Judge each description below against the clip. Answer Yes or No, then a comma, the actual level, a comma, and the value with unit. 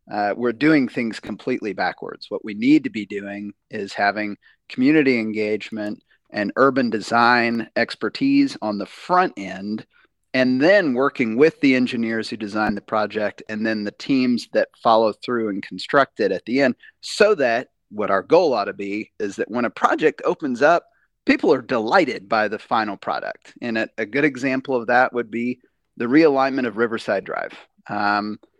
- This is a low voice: Yes, low, 115 Hz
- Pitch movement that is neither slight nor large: Yes, average, 4.1 semitones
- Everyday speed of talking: Yes, average, 175 wpm